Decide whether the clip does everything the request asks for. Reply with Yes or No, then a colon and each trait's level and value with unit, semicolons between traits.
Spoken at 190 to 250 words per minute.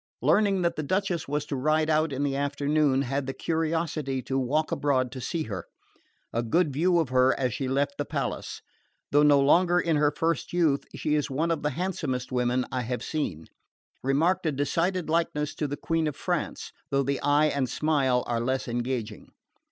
Yes: average, 195 wpm